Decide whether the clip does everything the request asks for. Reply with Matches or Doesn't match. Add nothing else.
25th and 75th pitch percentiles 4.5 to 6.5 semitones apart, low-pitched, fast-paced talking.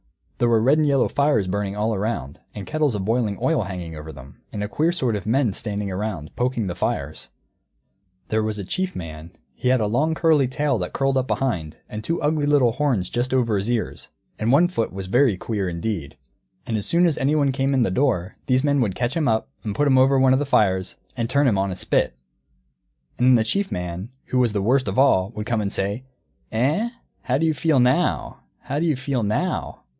Matches